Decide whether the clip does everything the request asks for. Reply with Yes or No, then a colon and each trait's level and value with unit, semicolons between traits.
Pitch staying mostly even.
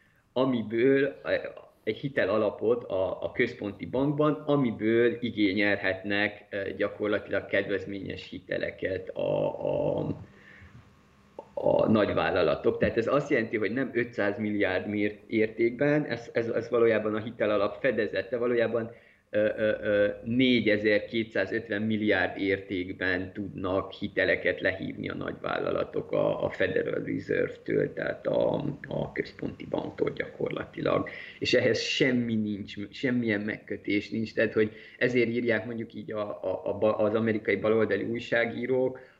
No: average, 3.6 semitones